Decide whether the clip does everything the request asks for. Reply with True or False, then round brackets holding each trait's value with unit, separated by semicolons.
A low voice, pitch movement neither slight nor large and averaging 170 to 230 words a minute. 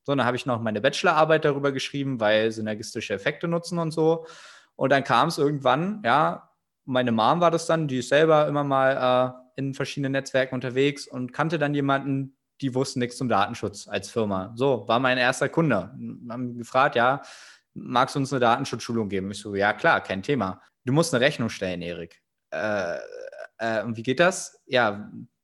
True (130 Hz; 3.7 semitones; 190 wpm)